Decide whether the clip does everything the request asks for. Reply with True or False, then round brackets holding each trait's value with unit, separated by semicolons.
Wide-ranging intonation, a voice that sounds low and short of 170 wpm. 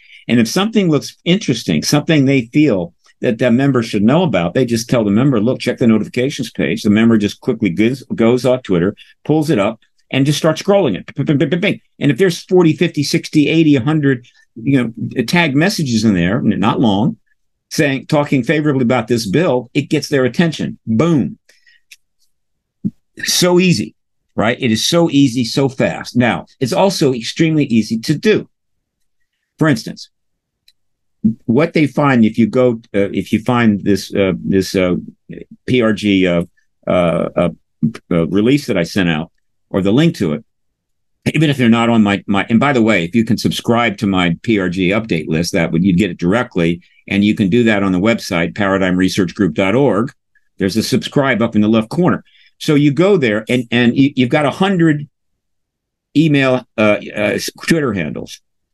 False (6.4 semitones; 125 Hz; 175 wpm)